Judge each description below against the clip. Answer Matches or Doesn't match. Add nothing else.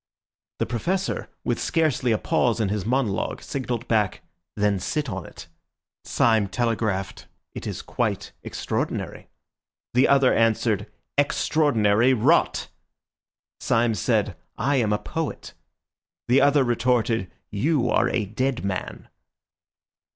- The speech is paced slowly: Matches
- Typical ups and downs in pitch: Matches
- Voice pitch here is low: Matches